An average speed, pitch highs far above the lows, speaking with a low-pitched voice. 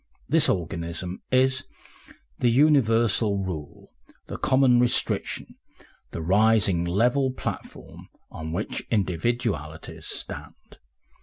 No: slow, 90 wpm; wide, 6.2 semitones; low, 110 Hz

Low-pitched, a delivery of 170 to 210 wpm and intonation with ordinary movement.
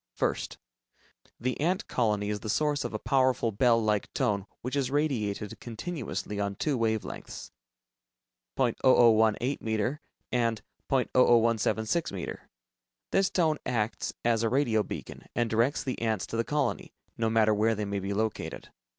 No: low, 115 Hz; average, 150 wpm; average, 3.3 semitones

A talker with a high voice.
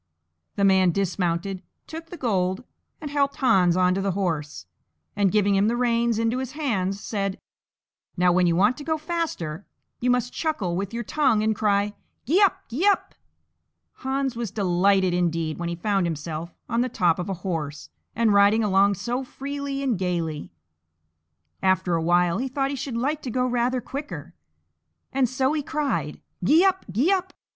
Yes: high, 210 Hz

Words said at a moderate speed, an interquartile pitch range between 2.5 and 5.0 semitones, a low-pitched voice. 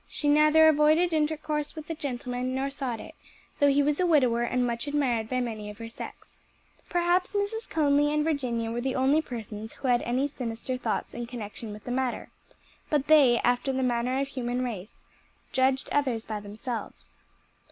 No: average, 185 wpm; average, 3.8 semitones; very high, 260 Hz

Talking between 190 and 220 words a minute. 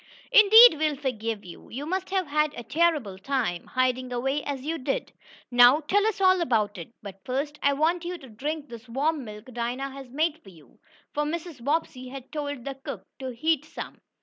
Yes: average, 200 wpm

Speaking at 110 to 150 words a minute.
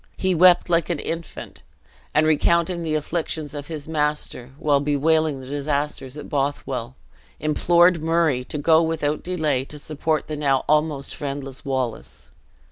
Yes: average, 145 wpm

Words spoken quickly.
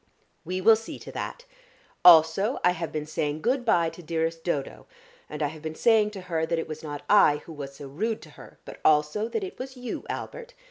Yes: fast, 225 wpm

